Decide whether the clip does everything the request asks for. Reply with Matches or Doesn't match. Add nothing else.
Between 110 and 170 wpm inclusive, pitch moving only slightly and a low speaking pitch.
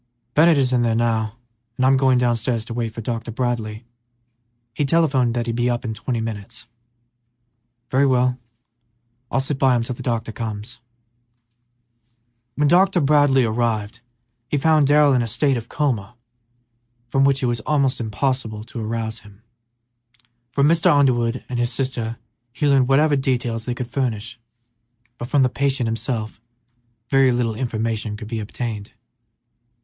Doesn't match